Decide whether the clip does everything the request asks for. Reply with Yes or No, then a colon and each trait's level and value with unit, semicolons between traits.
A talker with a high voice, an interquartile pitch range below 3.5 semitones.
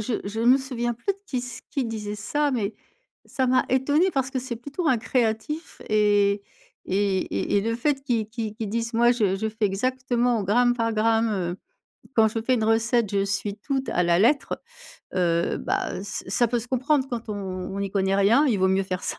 No: high, 225 Hz; average, 3.8 semitones